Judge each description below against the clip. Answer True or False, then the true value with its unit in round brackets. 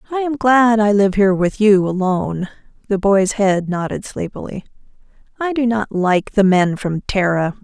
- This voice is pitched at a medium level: False (205 Hz)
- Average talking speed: True (175 wpm)